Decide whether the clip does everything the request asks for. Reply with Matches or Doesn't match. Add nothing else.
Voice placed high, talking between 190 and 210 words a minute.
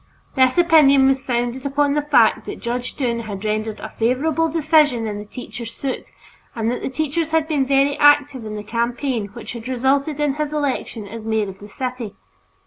Matches